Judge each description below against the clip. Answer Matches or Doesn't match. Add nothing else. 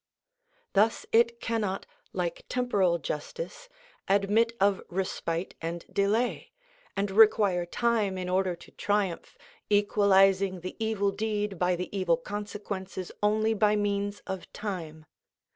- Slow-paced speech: Matches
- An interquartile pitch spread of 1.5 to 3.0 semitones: Matches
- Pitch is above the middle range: Matches